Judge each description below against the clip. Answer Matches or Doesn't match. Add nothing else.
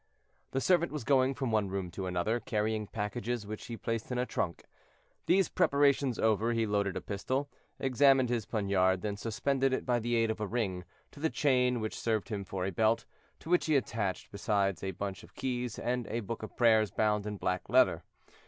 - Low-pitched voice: Matches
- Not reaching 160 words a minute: Doesn't match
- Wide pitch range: Doesn't match